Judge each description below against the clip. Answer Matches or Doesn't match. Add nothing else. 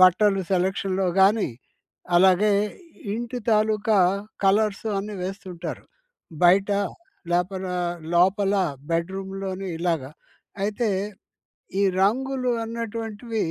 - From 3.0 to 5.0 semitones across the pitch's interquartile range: Doesn't match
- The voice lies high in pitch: Matches